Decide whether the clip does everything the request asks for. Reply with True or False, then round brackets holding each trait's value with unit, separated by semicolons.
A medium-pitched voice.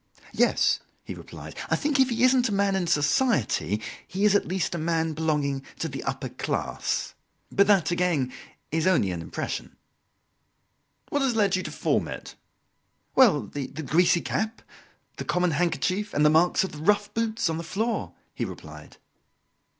True (175 Hz)